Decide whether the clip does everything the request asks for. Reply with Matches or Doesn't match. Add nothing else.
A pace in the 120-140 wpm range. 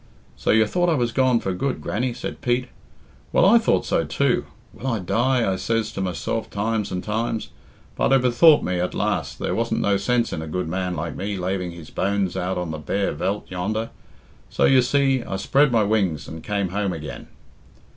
Doesn't match